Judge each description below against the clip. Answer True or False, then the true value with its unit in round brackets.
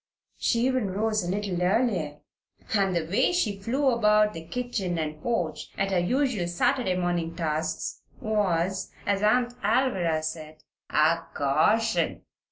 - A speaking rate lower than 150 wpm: True (140 wpm)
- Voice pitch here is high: True (195 Hz)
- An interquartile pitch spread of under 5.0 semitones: False (5.4 semitones)